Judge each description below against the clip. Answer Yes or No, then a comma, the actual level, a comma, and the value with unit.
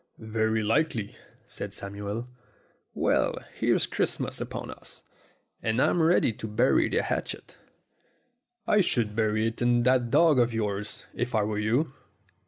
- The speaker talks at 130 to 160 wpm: Yes, average, 140 wpm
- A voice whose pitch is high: No, low, 115 Hz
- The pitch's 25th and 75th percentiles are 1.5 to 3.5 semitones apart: Yes, narrow, 2.6 semitones